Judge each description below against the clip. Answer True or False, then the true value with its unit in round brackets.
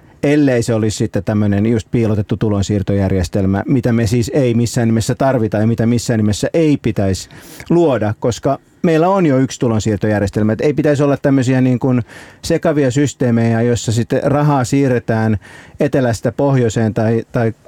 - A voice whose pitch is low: True (120 Hz)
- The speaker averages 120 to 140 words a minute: False (155 wpm)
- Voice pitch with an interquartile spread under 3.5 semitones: False (4.0 semitones)